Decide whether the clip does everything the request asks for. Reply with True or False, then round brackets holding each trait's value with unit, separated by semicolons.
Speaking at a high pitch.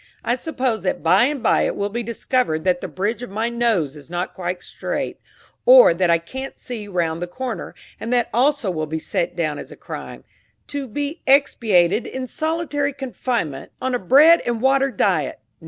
True (235 Hz)